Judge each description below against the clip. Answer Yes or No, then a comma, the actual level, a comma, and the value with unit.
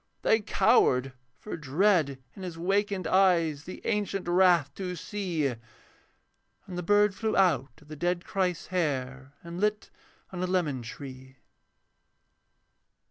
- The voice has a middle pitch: Yes, medium, 175 Hz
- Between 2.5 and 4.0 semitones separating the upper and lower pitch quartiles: No, average, 5.3 semitones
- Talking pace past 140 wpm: No, slow, 135 wpm